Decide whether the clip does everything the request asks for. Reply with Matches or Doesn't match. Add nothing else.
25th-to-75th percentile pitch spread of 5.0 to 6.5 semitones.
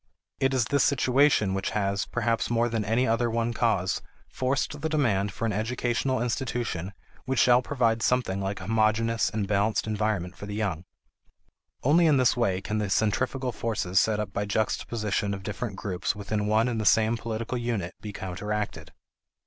Doesn't match